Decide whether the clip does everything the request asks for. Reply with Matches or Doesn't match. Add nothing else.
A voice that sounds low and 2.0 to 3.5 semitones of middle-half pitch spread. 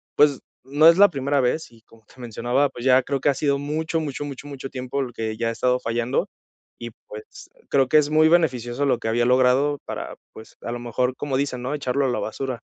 Matches